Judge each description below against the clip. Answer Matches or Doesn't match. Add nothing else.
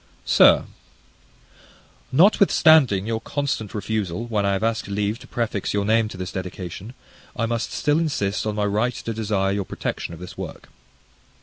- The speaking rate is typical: Matches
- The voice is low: Matches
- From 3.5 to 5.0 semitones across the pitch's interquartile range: Doesn't match